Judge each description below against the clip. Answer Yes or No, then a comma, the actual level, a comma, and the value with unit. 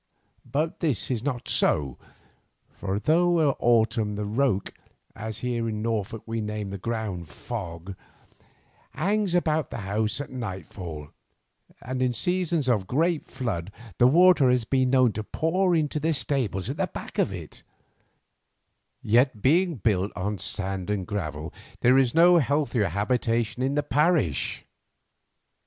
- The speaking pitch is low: Yes, low, 120 Hz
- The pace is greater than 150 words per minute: No, average, 145 wpm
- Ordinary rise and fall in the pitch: No, wide, 6.0 semitones